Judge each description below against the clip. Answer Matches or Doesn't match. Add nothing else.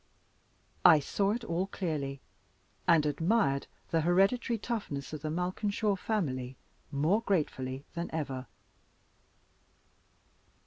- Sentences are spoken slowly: Matches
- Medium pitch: Matches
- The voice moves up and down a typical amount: Doesn't match